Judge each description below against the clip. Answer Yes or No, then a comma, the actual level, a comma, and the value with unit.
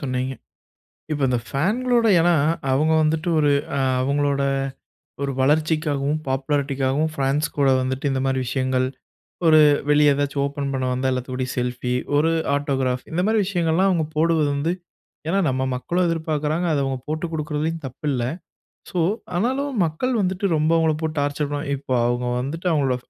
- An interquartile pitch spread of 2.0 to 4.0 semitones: Yes, average, 3.3 semitones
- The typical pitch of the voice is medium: Yes, medium, 145 Hz